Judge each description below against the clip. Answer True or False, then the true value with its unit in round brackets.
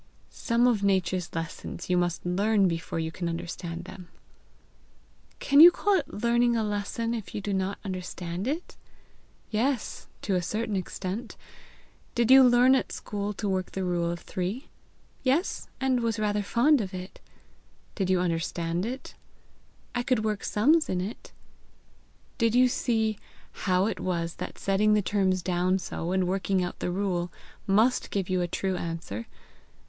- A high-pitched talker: True (195 Hz)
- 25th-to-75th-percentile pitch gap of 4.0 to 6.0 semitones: True (4.3 semitones)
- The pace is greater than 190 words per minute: False (165 wpm)